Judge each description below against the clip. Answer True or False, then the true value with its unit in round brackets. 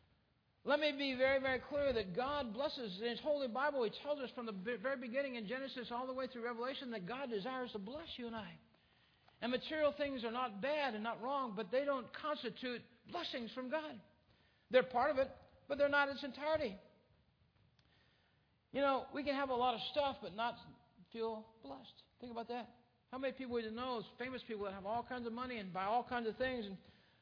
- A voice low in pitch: False (255 Hz)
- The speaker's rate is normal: False (215 wpm)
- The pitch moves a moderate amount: True (3.0 semitones)